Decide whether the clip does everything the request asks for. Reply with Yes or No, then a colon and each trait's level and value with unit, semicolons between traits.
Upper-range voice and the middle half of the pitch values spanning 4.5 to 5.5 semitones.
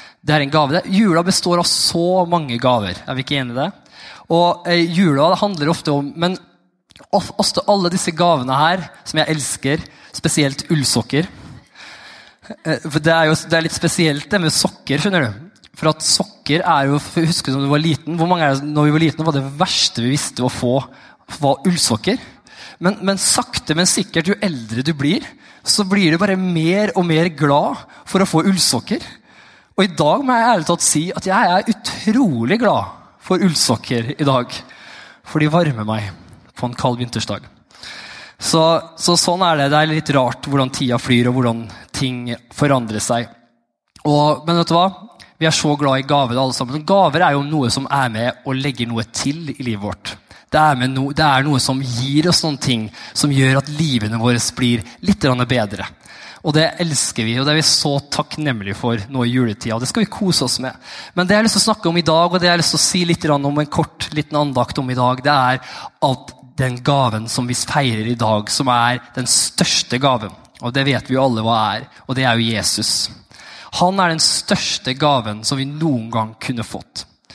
No: medium, 145 Hz; average, 5.1 semitones